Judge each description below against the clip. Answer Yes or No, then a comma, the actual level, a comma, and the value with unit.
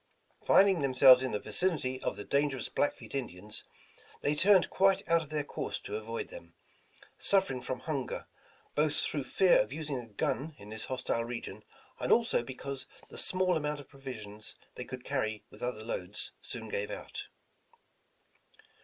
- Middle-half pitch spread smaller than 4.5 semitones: No, average, 4.9 semitones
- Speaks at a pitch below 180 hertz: Yes, low, 135 Hz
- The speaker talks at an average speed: Yes, average, 160 wpm